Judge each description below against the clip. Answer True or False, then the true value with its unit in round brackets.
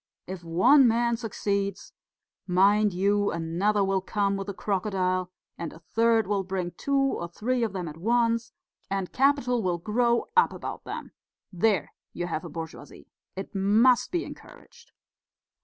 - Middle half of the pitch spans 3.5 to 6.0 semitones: True (4.2 semitones)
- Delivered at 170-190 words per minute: False (155 wpm)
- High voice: True (200 Hz)